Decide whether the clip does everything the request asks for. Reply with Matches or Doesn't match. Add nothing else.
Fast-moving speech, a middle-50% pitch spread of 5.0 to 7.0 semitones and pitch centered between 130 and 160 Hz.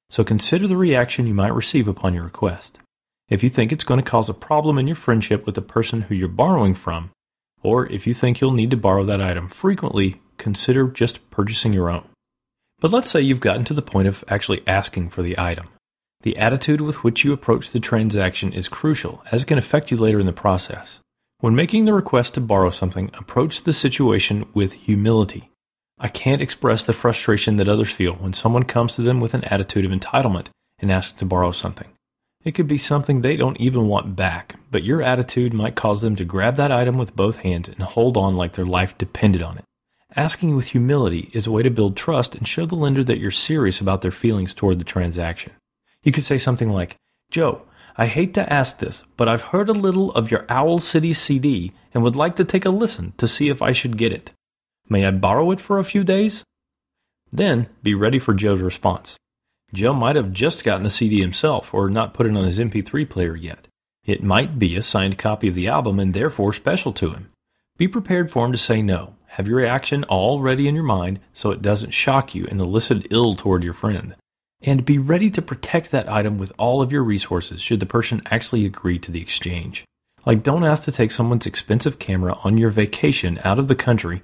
Doesn't match